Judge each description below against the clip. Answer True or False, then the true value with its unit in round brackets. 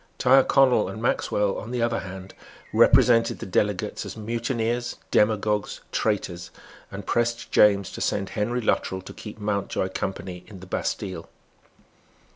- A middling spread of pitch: True (3.4 semitones)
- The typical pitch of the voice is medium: False (105 Hz)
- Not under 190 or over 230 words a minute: False (135 wpm)